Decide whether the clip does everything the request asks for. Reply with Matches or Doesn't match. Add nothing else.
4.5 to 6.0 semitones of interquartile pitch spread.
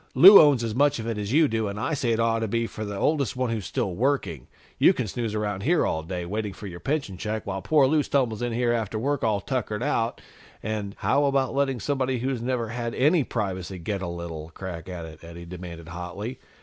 Matches